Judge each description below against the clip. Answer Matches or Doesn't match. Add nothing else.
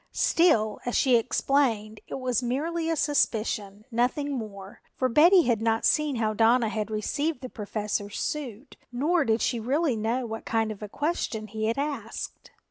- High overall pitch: Matches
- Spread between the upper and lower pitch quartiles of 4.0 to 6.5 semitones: Matches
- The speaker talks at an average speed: Matches